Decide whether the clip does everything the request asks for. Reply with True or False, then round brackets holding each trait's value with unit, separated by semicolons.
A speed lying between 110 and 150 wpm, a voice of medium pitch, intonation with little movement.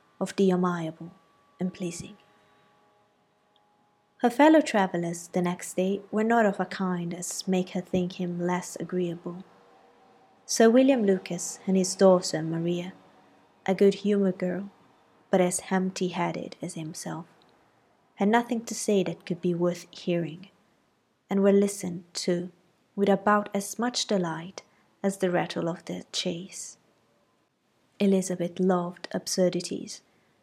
True (130 wpm; 180 Hz; 2.2 semitones)